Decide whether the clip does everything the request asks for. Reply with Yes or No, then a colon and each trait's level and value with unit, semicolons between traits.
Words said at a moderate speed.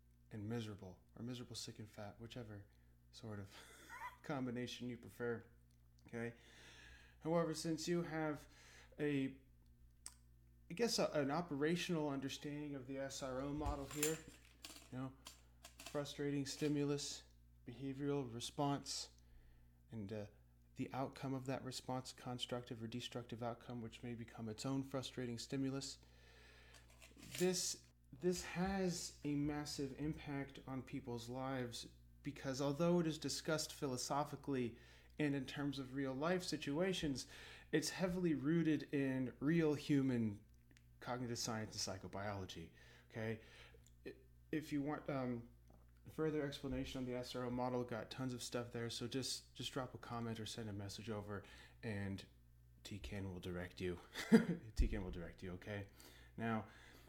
No: slow, 130 wpm